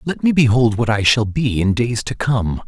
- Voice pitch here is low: Yes, low, 115 Hz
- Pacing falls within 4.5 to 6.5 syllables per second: Yes, 4.7 syllables/s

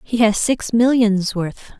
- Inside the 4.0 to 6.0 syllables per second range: No, 3.6 syllables/s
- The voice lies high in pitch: Yes, high, 220 Hz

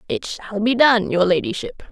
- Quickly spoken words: No, average, 190 wpm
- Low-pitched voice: No, high, 225 Hz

